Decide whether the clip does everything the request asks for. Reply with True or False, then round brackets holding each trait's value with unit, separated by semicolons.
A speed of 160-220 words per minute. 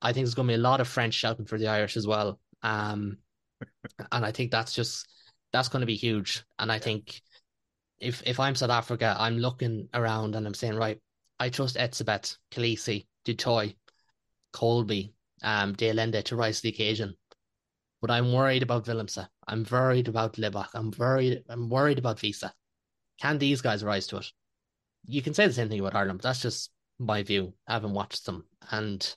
True (195 wpm)